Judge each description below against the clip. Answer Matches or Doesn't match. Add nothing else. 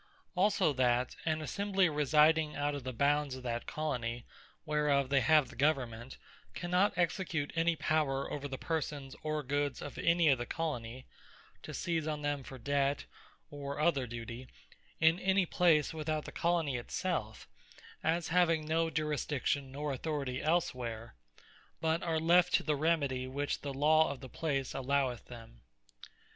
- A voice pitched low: Doesn't match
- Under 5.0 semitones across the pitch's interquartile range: Matches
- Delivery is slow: Doesn't match